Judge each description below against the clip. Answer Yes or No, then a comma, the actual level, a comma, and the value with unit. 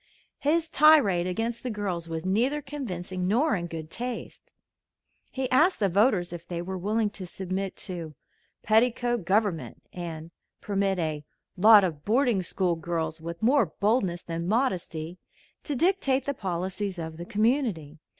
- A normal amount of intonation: No, wide, 5.7 semitones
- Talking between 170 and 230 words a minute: No, average, 150 wpm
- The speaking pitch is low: No, high, 195 Hz